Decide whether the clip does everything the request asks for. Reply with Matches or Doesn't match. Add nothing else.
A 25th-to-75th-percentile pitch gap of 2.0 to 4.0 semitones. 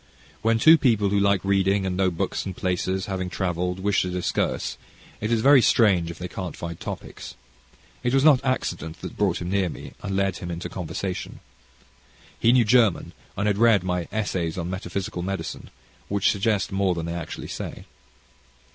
Matches